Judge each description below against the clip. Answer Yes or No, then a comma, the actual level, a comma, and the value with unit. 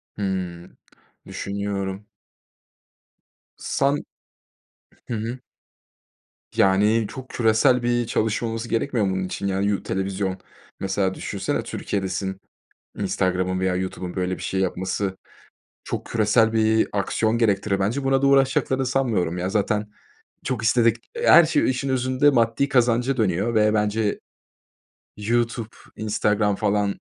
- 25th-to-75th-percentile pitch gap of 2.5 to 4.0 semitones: Yes, average, 3.7 semitones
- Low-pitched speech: Yes, low, 105 Hz